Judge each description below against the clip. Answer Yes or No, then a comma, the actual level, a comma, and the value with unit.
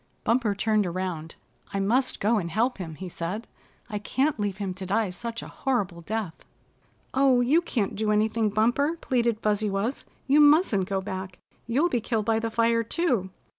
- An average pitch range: Yes, average, 3.7 semitones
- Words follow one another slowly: No, average, 180 wpm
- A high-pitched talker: Yes, high, 220 Hz